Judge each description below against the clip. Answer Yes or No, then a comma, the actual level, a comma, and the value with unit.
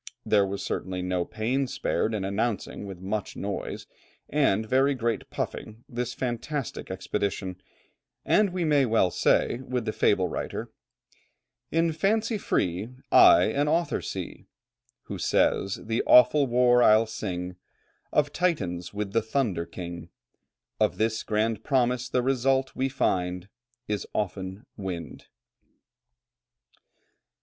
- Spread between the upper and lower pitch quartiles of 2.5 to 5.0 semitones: No, wide, 5.6 semitones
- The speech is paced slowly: Yes, slow, 125 wpm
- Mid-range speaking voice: No, low, 110 Hz